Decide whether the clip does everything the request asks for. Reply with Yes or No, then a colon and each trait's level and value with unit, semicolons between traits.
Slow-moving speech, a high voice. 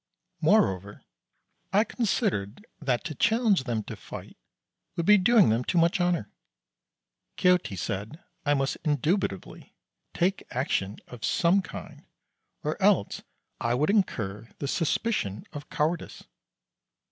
No: slow, 125 wpm; medium, 150 Hz